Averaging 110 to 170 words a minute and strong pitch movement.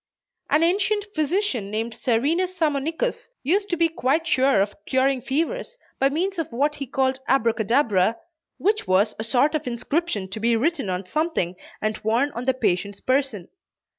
Yes: average, 165 wpm; wide, 6.5 semitones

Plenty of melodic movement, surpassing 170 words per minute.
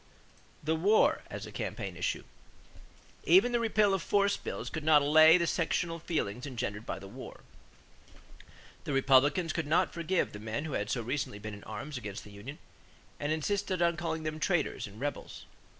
Yes: wide, 5.9 semitones; average, 180 wpm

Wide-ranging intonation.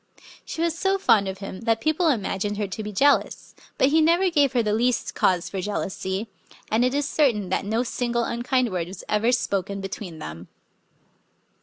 Yes: wide, 5.7 semitones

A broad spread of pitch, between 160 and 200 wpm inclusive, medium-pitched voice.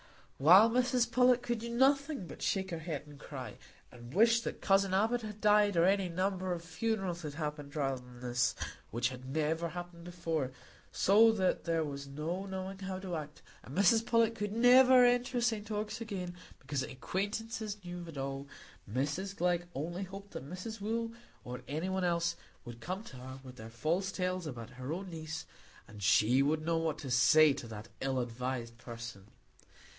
Yes: wide, 6.9 semitones; average, 185 wpm; medium, 175 Hz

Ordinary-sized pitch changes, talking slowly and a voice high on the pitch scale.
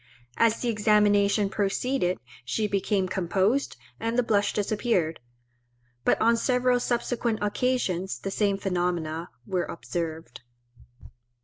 Yes: average, 4.0 semitones; slow, 110 wpm; high, 205 Hz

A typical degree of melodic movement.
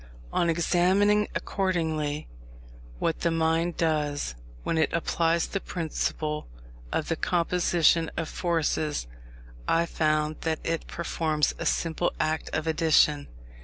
No: narrow, 1.7 semitones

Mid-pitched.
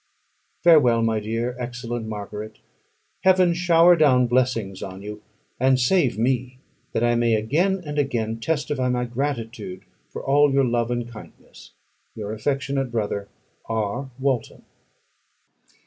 No: low, 120 Hz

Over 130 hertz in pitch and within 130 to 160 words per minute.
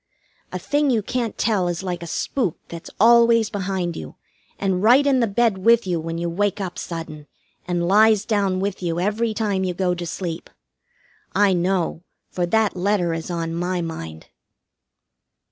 No: high, 190 Hz; average, 175 wpm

